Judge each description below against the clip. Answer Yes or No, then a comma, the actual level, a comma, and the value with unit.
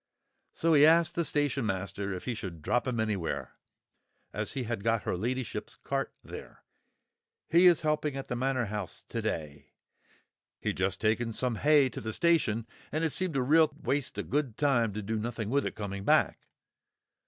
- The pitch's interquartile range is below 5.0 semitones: No, wide, 5.6 semitones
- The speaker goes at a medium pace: Yes, average, 185 wpm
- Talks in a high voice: No, low, 120 Hz